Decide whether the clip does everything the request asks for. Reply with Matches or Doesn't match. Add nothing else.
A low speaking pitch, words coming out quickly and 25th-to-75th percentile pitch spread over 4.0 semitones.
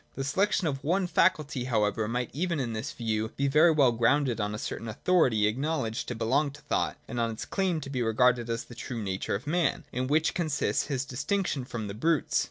Matches